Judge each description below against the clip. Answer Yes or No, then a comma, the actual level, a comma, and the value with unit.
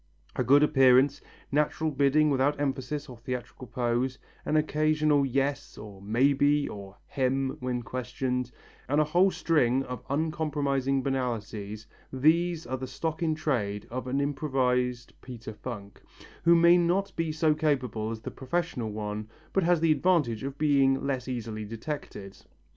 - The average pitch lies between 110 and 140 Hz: Yes, low, 135 Hz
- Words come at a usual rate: Yes, average, 150 wpm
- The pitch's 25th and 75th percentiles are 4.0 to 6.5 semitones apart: No, average, 3.6 semitones